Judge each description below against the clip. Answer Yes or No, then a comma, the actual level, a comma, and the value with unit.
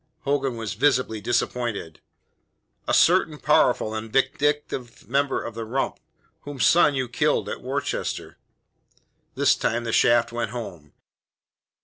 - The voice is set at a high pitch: No, low, 120 Hz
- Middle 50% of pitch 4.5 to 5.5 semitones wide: No, average, 3.3 semitones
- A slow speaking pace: Yes, slow, 125 wpm